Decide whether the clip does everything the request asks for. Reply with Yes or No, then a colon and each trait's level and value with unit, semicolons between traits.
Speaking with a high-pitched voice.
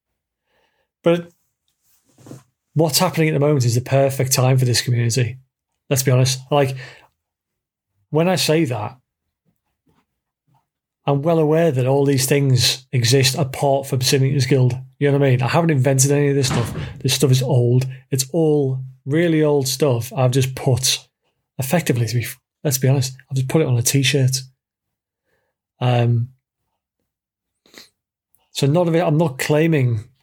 No: low, 135 Hz